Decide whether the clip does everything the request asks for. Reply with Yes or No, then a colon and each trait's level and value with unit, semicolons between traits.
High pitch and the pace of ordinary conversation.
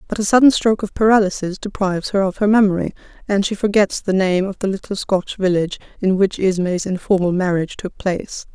Yes: high, 195 Hz; average, 195 wpm